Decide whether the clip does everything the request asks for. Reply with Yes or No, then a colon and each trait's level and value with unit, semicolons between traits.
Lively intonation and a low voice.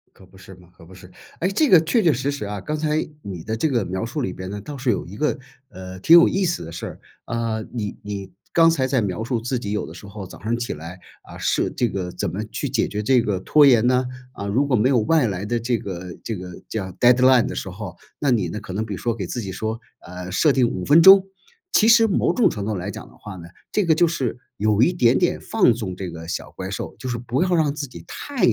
Yes: wide, 6.4 semitones; low, 115 Hz